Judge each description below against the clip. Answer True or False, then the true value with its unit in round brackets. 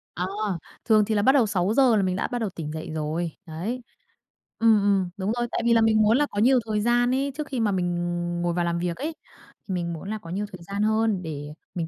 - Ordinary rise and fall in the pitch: True (4.6 semitones)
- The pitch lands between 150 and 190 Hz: False (205 Hz)